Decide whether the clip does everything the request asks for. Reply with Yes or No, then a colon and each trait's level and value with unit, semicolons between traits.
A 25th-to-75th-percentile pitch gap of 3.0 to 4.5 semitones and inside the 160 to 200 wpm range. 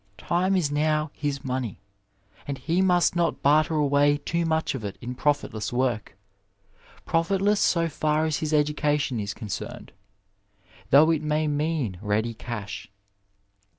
No: average, 4.2 semitones; average, 145 wpm